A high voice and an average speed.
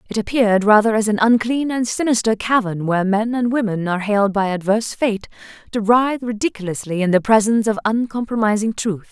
Yes: high, 220 Hz; average, 180 wpm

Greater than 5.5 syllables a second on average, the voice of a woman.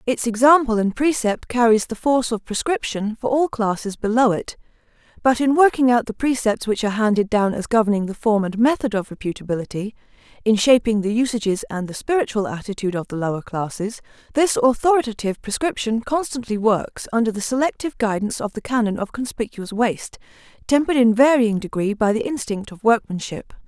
Yes: 5.9 syllables/s; female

